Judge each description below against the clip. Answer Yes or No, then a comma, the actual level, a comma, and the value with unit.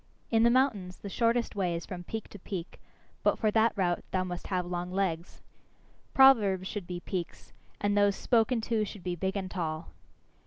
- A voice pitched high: Yes, high, 195 Hz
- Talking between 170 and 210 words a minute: Yes, average, 190 wpm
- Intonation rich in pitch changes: No, average, 3.6 semitones